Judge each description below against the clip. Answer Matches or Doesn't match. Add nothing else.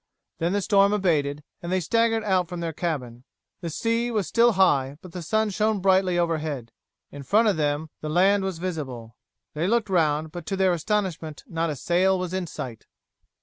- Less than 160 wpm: Doesn't match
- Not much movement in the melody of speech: Doesn't match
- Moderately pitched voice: Matches